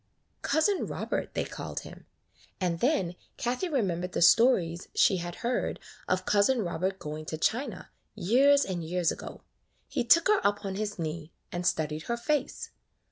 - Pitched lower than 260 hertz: Yes, high, 190 Hz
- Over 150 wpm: Yes, average, 160 wpm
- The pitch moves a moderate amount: No, wide, 6.3 semitones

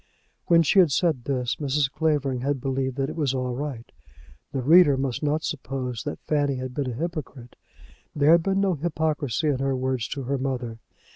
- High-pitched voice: No, medium, 140 Hz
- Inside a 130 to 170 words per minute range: No, average, 195 wpm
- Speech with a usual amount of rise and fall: Yes, average, 3.1 semitones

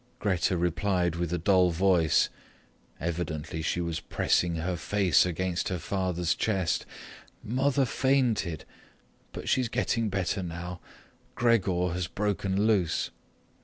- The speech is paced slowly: Yes, slow, 120 wpm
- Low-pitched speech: Yes, very low, 90 Hz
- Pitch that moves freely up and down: No, average, 3.1 semitones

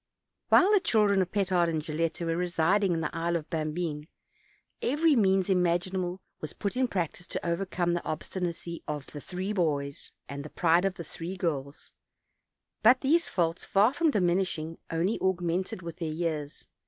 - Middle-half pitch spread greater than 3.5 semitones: No, average, 2.8 semitones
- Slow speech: No, average, 175 wpm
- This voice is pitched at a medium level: Yes, medium, 175 Hz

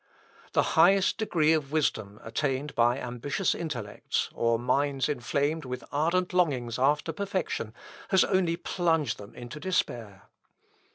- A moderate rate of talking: No, slow, 125 wpm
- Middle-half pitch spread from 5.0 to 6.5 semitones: Yes, wide, 5.5 semitones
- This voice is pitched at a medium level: Yes, medium, 145 Hz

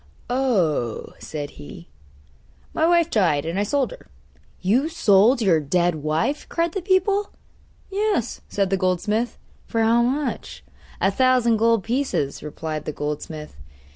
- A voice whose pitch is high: Yes, high, 215 Hz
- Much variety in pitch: Yes, wide, 9.0 semitones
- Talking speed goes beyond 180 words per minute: No, average, 140 wpm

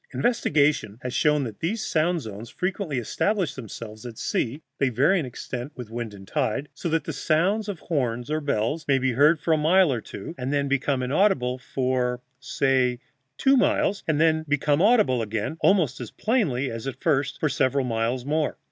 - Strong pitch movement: No, average, 4.5 semitones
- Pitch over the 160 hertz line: No, medium, 140 Hz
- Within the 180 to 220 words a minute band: Yes, average, 190 wpm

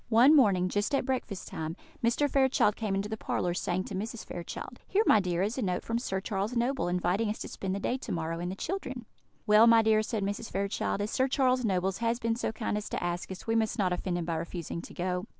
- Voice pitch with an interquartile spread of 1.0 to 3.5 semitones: No, average, 4.2 semitones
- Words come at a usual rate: No, fast, 250 wpm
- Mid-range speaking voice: No, high, 210 Hz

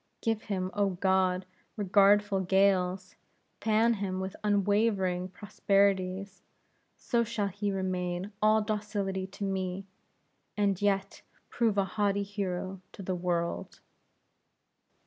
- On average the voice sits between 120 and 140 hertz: No, high, 195 Hz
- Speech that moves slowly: Yes, slow, 110 wpm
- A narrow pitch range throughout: Yes, narrow, 1.7 semitones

